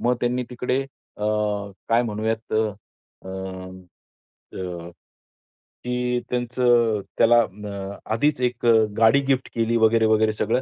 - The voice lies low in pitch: Yes, low, 115 Hz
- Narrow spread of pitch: Yes, narrow, 2.2 semitones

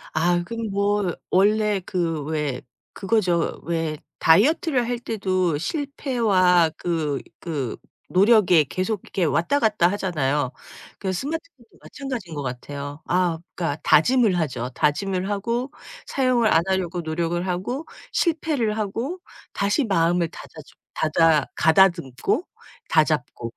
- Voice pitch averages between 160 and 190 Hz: Yes, medium, 185 Hz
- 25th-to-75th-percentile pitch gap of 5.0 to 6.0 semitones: Yes, wide, 5.6 semitones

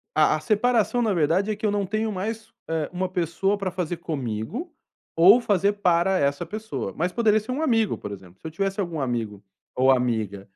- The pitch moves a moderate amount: No, wide, 7.2 semitones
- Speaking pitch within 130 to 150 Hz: No, medium, 180 Hz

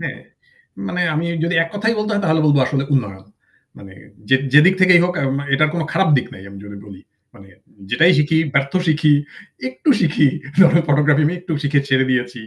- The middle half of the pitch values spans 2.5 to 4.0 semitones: No, average, 4.5 semitones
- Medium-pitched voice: Yes, medium, 150 Hz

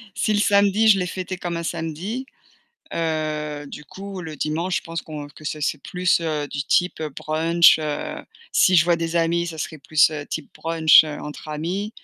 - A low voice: No, medium, 165 Hz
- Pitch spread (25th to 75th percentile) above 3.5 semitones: No, average, 2.8 semitones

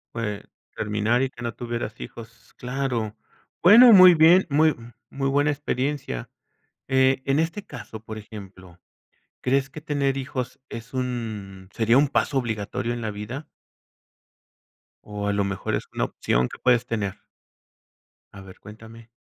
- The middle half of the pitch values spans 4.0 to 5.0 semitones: Yes, average, 4.5 semitones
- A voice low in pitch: Yes, low, 120 Hz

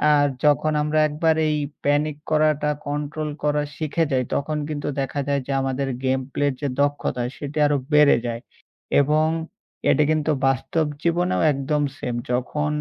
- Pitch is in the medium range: Yes, medium, 145 Hz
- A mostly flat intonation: Yes, narrow, 1.6 semitones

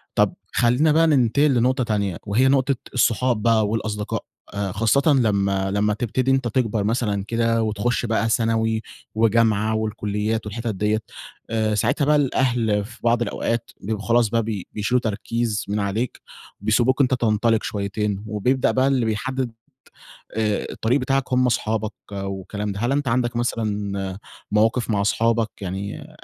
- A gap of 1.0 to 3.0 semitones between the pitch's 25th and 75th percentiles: Yes, average, 2.7 semitones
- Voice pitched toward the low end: Yes, low, 110 Hz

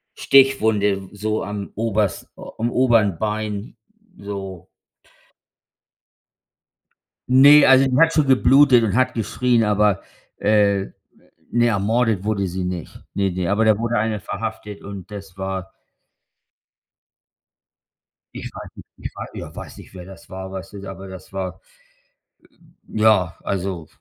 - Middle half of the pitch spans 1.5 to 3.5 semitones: Yes, average, 2.9 semitones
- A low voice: Yes, low, 105 Hz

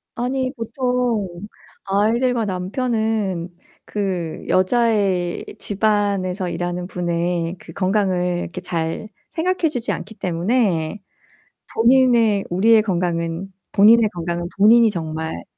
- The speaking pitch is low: No, high, 195 Hz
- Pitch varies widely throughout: No, average, 4.5 semitones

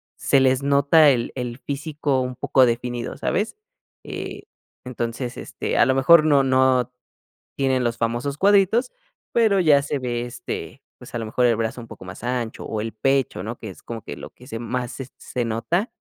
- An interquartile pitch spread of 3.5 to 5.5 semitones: No, average, 3.0 semitones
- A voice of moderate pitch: No, low, 125 Hz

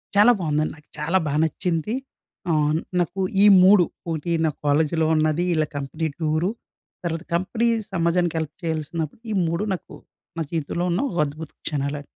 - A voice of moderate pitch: Yes, medium, 160 Hz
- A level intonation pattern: Yes, narrow, 2.3 semitones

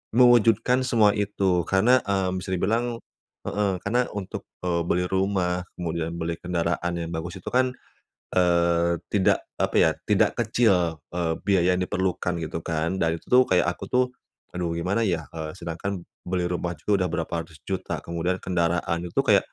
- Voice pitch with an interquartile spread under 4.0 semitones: Yes, average, 2.9 semitones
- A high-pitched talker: No, very low, 90 Hz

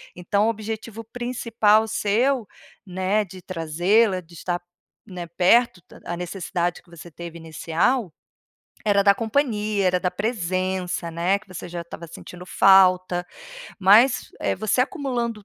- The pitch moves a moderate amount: Yes, average, 3.8 semitones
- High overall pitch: Yes, high, 195 Hz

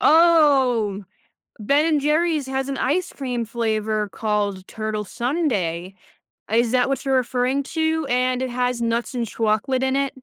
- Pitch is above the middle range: Yes, very high, 250 Hz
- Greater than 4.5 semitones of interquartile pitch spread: No, average, 4.2 semitones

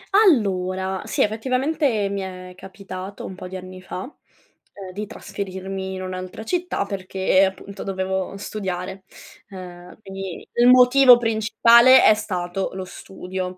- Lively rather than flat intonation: No, average, 2.7 semitones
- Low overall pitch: No, high, 195 Hz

